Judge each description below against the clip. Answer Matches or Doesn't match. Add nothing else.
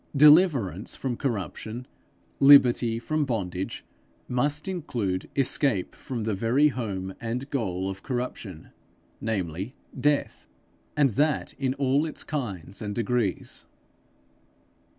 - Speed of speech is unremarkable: Doesn't match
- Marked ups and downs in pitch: Matches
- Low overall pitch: Matches